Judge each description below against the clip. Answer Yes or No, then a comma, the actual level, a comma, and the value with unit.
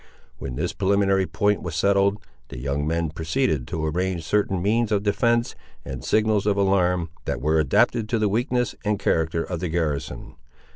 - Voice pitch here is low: Yes, very low, 95 Hz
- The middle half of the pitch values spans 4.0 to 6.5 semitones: Yes, average, 4.4 semitones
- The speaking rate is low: No, average, 175 wpm